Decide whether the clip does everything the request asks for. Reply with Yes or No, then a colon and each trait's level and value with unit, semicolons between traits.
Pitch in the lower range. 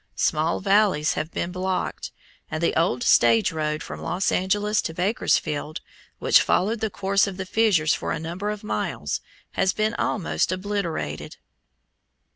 No: medium, 185 Hz